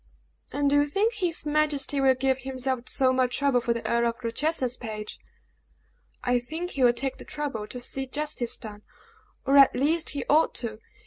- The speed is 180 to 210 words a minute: Yes, average, 190 wpm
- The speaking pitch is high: Yes, very high, 265 Hz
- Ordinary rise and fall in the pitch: Yes, average, 3.3 semitones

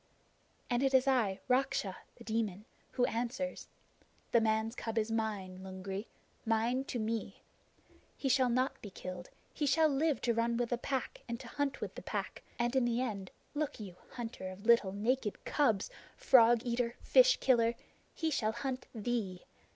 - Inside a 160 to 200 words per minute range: Yes, average, 170 wpm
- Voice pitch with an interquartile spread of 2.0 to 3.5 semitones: Yes, average, 3.1 semitones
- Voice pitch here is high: Yes, high, 235 Hz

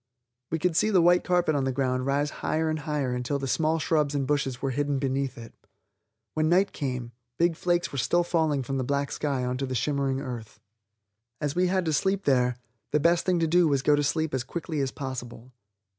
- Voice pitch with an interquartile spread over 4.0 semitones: No, average, 3.7 semitones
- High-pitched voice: No, medium, 145 Hz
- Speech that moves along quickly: Yes, fast, 220 wpm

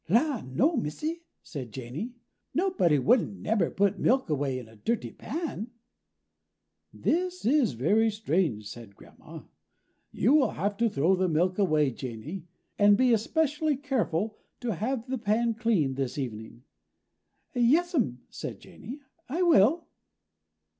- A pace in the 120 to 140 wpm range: Yes, slow, 135 wpm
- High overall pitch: Yes, high, 210 Hz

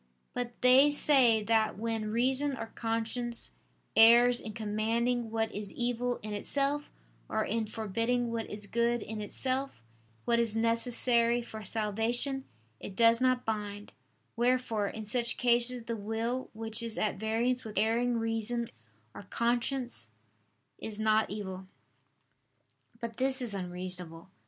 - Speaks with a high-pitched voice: Yes, high, 230 Hz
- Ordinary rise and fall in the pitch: No, narrow, 2.0 semitones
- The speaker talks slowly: Yes, slow, 130 wpm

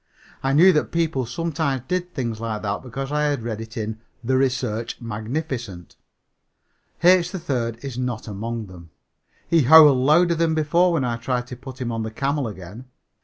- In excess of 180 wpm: No, average, 175 wpm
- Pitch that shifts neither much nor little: Yes, average, 5.0 semitones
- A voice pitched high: No, low, 130 Hz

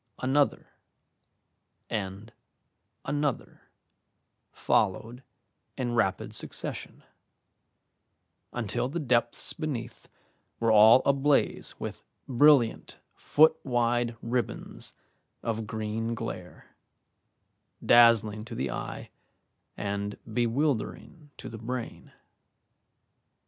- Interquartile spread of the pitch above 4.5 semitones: No, average, 2.9 semitones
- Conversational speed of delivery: No, slow, 80 wpm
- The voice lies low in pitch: Yes, low, 120 Hz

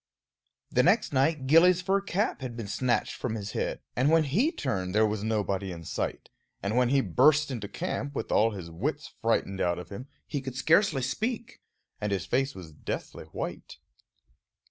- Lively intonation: Yes, wide, 7.3 semitones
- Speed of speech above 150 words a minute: Yes, average, 185 wpm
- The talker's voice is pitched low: Yes, low, 125 Hz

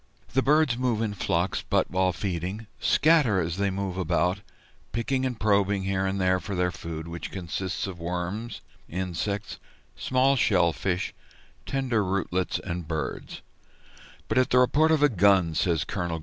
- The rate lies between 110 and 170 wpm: Yes, average, 160 wpm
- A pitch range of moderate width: Yes, average, 4.7 semitones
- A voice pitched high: No, very low, 95 Hz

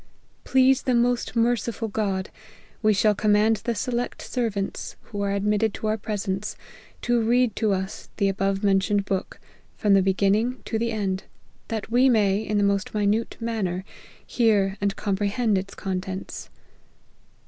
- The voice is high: Yes, high, 210 Hz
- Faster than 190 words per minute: No, average, 150 wpm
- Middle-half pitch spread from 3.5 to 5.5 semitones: No, narrow, 2.6 semitones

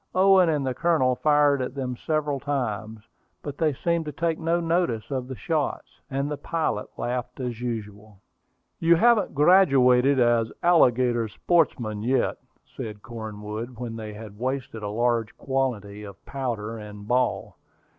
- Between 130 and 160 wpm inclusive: Yes, average, 150 wpm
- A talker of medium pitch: No, low, 125 Hz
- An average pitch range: Yes, average, 5.0 semitones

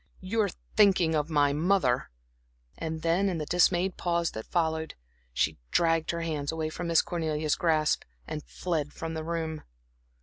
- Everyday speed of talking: Yes, average, 160 wpm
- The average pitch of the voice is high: No, medium, 160 Hz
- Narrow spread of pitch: Yes, narrow, 2.0 semitones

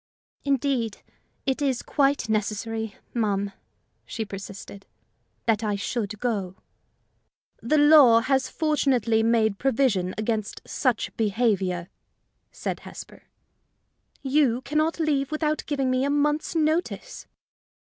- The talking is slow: Yes, slow, 110 wpm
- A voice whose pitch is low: No, high, 240 Hz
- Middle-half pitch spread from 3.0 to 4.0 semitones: No, average, 4.9 semitones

